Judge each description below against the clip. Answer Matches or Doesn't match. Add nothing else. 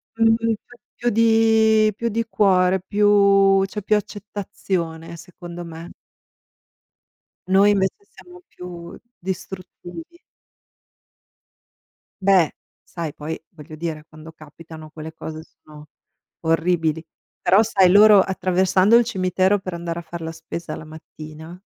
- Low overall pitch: Doesn't match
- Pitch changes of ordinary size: Matches